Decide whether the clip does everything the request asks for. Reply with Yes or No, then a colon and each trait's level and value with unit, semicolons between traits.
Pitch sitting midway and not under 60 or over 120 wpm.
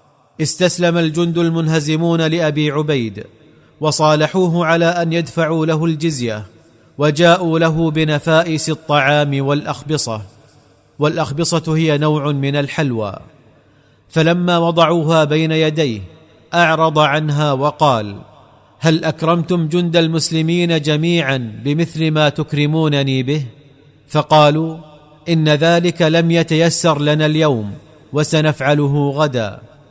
Yes: medium, 155 Hz; average, 90 wpm